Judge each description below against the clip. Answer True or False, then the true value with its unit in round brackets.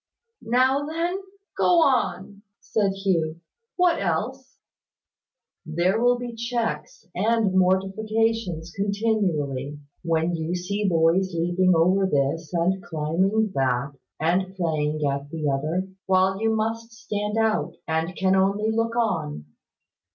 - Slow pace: True (120 wpm)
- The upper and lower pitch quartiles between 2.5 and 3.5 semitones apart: False (5.2 semitones)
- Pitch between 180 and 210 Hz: True (190 Hz)